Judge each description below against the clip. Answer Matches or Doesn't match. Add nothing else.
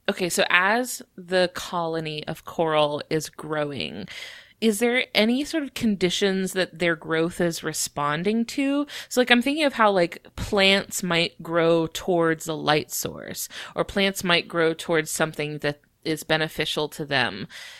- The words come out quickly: Doesn't match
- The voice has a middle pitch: Matches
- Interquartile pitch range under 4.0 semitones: Doesn't match